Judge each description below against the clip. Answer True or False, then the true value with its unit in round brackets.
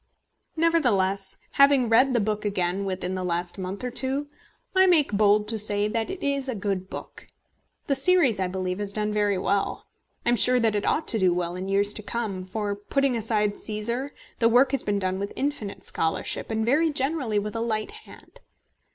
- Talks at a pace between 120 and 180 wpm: False (200 wpm)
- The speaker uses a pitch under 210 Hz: False (215 Hz)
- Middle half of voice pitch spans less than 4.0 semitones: False (4.7 semitones)